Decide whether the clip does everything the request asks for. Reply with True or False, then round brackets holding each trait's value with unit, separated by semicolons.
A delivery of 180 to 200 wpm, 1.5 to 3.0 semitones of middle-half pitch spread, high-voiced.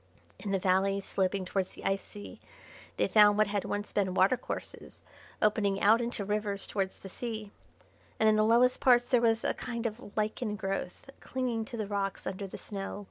True (190 wpm; 2.4 semitones; 210 Hz)